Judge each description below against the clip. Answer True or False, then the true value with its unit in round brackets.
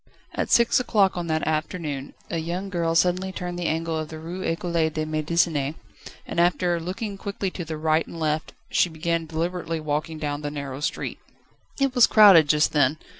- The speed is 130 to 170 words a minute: False (185 wpm)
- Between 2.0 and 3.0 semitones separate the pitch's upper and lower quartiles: True (2.5 semitones)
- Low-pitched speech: False (165 Hz)